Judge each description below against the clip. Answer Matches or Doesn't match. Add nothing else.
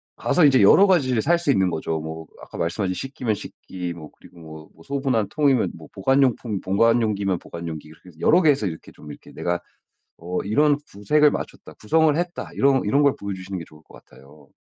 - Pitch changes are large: Matches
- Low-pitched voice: Matches